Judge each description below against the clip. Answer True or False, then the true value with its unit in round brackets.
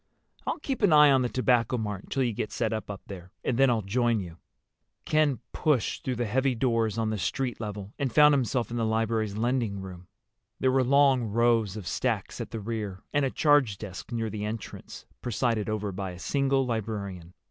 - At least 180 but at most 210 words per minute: True (200 wpm)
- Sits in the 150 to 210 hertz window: False (115 Hz)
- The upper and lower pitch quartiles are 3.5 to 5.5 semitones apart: True (3.9 semitones)